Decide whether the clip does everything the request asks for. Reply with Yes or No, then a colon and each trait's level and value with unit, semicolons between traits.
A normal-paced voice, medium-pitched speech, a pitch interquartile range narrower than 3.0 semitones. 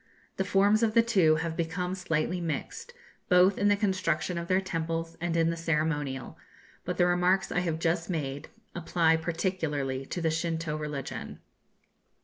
Yes: average, 160 wpm; medium, 170 Hz; narrow, 2.4 semitones